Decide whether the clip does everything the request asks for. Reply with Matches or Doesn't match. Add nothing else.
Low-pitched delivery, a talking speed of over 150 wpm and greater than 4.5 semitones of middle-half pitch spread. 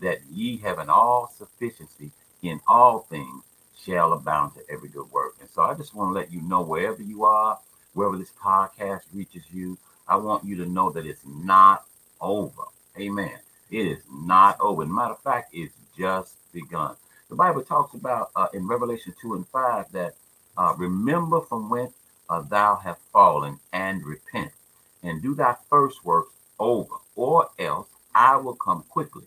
Matches